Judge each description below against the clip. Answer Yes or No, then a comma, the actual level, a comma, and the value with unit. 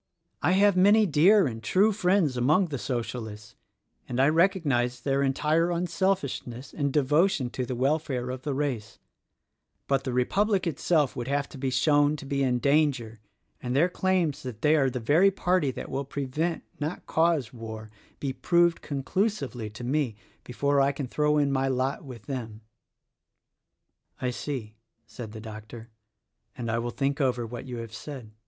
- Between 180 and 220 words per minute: No, average, 170 wpm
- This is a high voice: No, medium, 140 Hz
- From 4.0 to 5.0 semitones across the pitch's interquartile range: Yes, average, 4.4 semitones